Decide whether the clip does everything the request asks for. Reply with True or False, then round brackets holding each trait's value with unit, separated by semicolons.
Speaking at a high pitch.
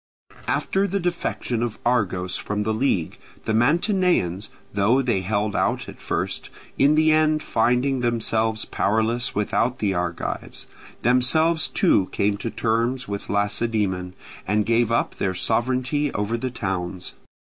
False (115 Hz)